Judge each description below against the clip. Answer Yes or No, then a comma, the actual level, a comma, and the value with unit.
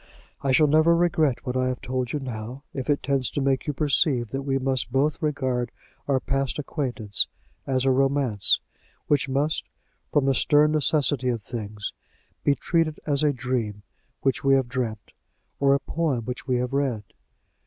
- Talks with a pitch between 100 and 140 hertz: Yes, low, 135 Hz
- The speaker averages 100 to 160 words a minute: No, average, 175 wpm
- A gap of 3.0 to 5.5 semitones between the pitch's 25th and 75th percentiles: No, narrow, 2.5 semitones